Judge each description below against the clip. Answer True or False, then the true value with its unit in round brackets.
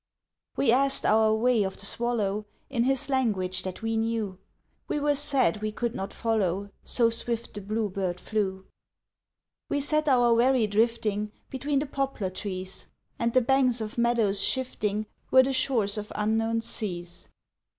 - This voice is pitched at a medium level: False (225 Hz)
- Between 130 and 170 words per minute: True (160 wpm)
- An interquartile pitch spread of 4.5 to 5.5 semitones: False (3.8 semitones)